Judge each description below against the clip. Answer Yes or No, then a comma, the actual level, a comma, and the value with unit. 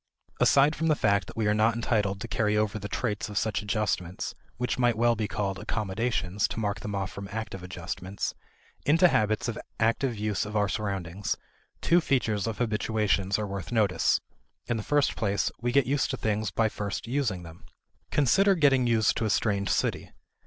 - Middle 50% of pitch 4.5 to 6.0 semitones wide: No, average, 2.9 semitones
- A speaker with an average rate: Yes, average, 190 wpm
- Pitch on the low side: Yes, low, 110 Hz